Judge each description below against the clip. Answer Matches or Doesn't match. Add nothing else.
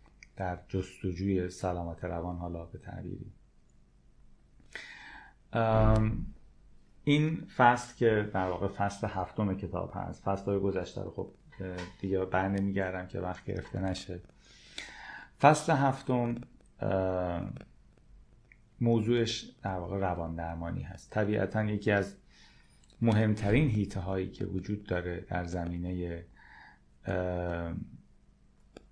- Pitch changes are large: Doesn't match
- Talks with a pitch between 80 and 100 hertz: Matches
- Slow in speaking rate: Matches